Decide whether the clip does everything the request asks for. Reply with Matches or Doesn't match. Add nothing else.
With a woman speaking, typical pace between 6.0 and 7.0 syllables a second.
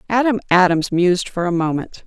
Doesn't match